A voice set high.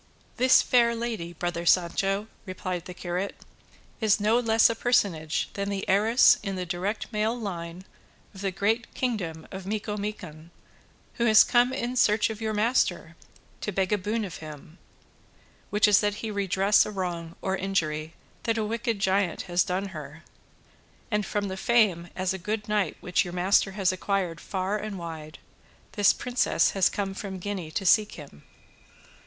Yes: high, 195 Hz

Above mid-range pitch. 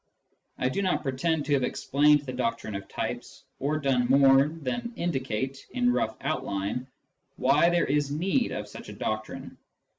No: medium, 140 Hz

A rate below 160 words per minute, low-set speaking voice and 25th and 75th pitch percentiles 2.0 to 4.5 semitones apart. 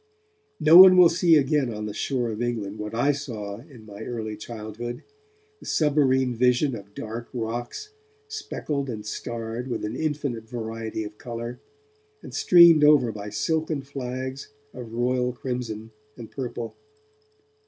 Yes: average, 145 wpm; low, 120 Hz; average, 4.0 semitones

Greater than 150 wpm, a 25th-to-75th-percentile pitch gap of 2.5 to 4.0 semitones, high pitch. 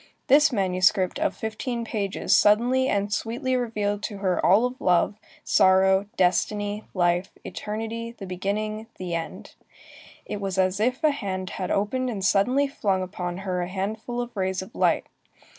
Yes: average, 160 wpm; average, 3.6 semitones; high, 205 Hz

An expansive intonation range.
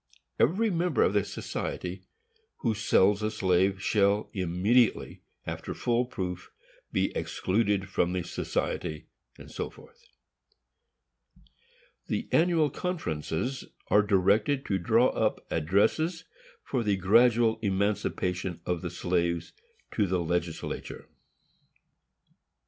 No: average, 4.6 semitones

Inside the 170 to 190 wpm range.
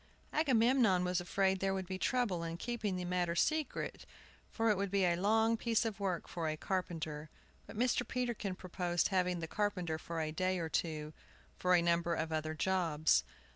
Yes: average, 185 wpm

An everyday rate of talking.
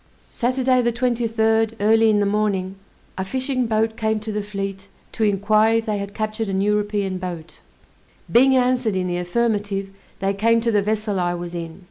Yes: average, 180 wpm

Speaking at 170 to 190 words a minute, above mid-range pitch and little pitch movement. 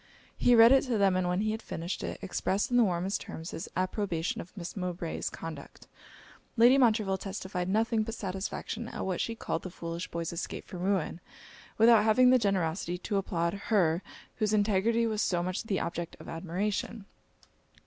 No: average, 180 wpm; high, 195 Hz; average, 3.9 semitones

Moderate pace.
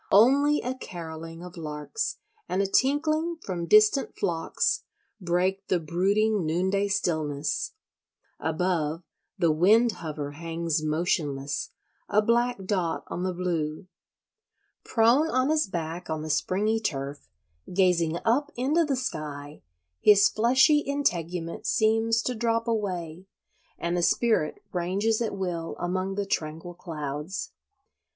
No: slow, 125 wpm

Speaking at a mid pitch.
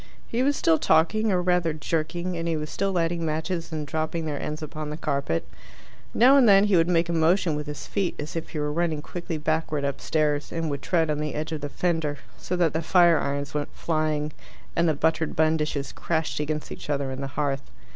Yes: medium, 160 Hz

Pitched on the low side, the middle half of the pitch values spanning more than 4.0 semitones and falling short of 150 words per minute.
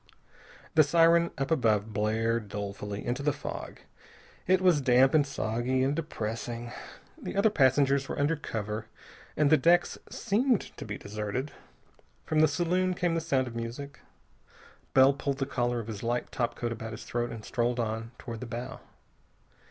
No: low, 130 Hz; average, 4.7 semitones; average, 165 wpm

